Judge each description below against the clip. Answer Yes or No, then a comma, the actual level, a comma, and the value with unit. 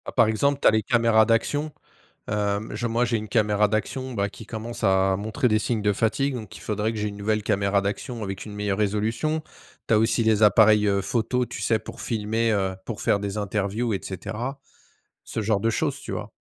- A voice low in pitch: Yes, low, 110 Hz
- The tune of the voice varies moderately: No, narrow, 2.0 semitones